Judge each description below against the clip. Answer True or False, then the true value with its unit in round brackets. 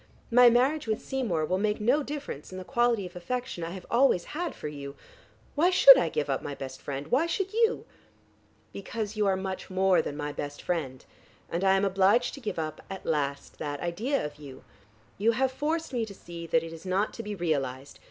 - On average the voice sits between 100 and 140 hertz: False (195 Hz)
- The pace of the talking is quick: True (215 wpm)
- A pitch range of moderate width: False (7.5 semitones)